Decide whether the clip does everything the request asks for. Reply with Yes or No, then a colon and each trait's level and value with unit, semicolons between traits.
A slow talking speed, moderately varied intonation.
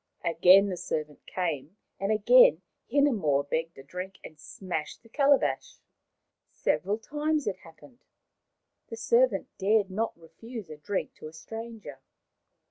No: slow, 130 wpm; wide, 5.9 semitones